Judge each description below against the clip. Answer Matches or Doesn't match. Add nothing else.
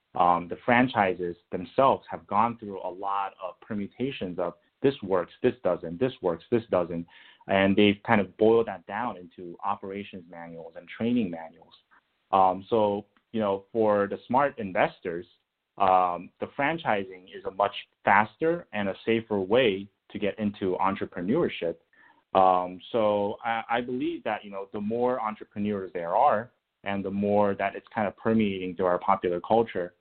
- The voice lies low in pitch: Matches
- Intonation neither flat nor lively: Matches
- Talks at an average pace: Matches